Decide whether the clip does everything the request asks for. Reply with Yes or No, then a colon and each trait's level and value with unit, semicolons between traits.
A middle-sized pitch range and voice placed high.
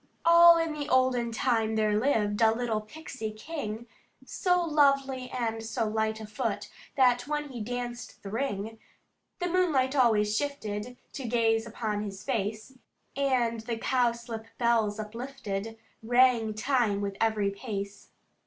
Yes: average, 3.3 semitones; high, 230 Hz